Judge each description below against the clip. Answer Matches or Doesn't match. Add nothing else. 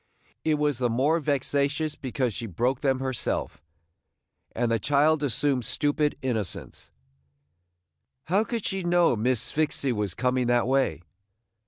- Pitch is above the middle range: Doesn't match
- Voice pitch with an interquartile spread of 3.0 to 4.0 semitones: Matches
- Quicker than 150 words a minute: Doesn't match